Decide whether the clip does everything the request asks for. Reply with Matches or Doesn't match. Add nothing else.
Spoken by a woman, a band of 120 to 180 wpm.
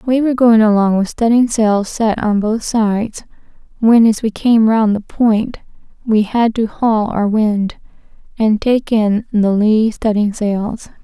Matches